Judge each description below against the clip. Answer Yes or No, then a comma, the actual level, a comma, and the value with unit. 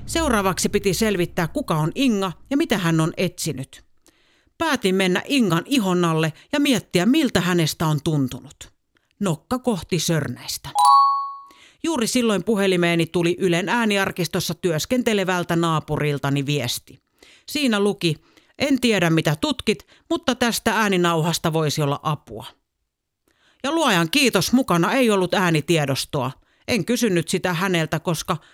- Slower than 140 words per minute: Yes, average, 120 wpm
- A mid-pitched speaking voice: Yes, medium, 180 Hz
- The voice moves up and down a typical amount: No, wide, 6.3 semitones